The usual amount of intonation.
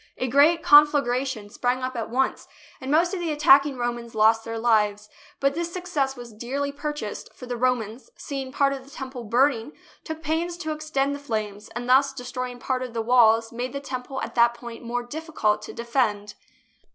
Yes: average, 3.3 semitones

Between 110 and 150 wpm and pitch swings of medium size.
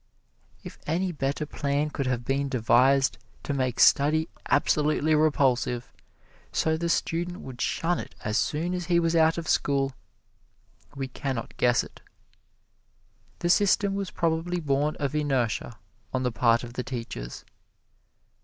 Yes: average, 145 wpm; average, 4.2 semitones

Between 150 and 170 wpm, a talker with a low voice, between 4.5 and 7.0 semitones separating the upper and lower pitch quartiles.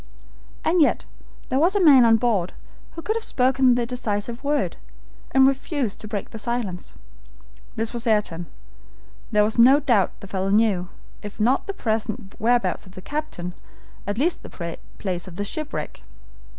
No: average, 165 wpm; high, 230 Hz; average, 4.8 semitones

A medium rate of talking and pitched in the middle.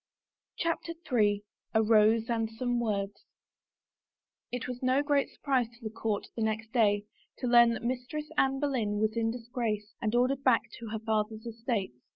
No: average, 170 wpm; high, 230 Hz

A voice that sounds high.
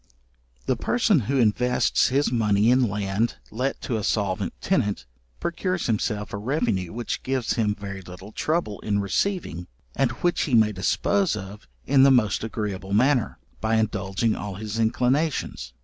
No: low, 110 Hz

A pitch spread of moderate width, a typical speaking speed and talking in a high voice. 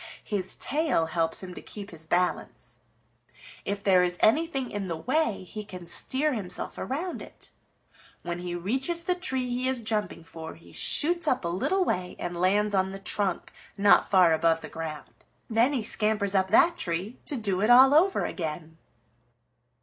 No: wide, 6.6 semitones; average, 175 wpm; high, 200 Hz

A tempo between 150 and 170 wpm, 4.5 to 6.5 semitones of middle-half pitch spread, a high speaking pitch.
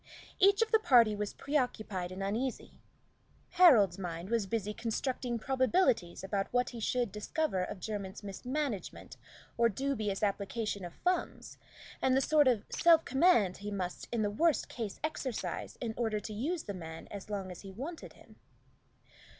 Yes: average, 160 wpm; average, 5.2 semitones; high, 225 Hz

